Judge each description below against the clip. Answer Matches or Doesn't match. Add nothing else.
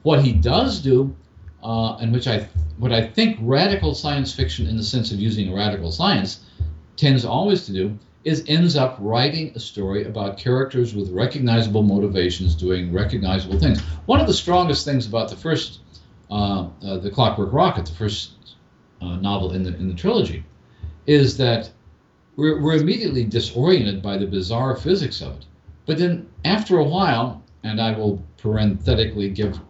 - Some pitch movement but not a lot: Doesn't match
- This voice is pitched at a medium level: Doesn't match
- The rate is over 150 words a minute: Matches